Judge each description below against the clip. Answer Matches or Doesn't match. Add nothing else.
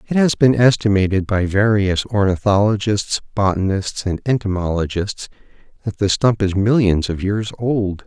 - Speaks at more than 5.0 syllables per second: Doesn't match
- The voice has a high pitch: Doesn't match